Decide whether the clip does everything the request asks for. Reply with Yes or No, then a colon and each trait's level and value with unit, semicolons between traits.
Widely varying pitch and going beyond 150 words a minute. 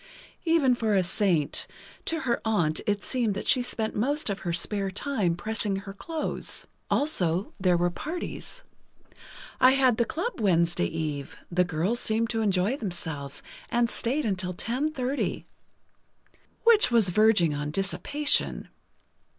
No: wide, 6.1 semitones; slow, 135 wpm